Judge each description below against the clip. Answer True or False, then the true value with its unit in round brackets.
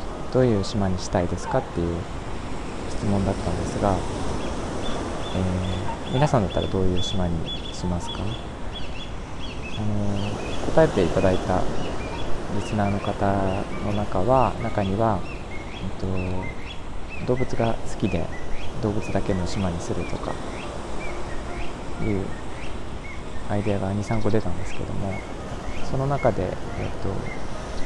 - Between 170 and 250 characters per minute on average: True (240 characters per minute)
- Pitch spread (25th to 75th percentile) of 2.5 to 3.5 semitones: True (2.9 semitones)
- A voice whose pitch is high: False (95 Hz)